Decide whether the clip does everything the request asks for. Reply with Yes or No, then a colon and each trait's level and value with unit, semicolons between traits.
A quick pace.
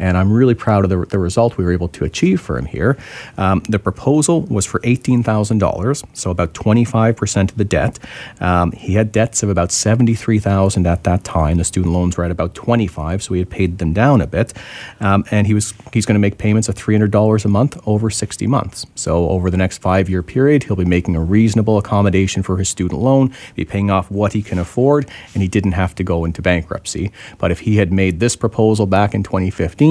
Yes: fast, 225 wpm